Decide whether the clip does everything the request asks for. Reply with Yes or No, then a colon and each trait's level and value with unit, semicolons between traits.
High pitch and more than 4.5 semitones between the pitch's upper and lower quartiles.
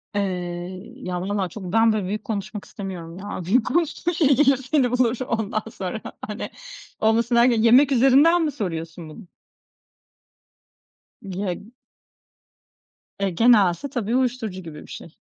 Yes: high, 215 Hz; average, 5.1 semitones